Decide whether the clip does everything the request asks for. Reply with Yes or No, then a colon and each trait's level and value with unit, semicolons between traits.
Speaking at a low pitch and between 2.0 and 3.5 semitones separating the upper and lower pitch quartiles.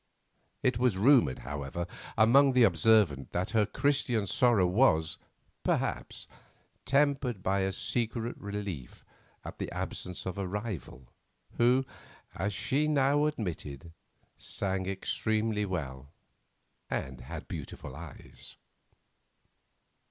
No: low, 105 Hz; wide, 5.6 semitones